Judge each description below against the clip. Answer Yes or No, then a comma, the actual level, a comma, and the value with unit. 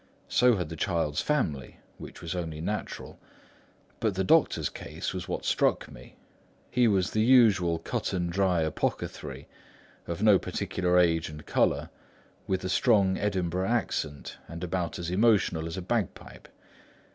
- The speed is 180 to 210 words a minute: No, average, 150 wpm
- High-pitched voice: No, very low, 90 Hz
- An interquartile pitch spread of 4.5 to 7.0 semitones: No, average, 3.7 semitones